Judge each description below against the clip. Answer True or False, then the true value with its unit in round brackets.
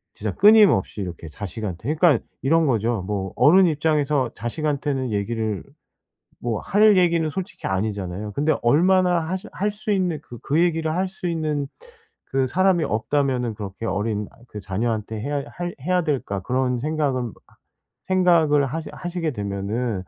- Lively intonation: True (7.5 semitones)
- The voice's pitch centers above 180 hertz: False (140 Hz)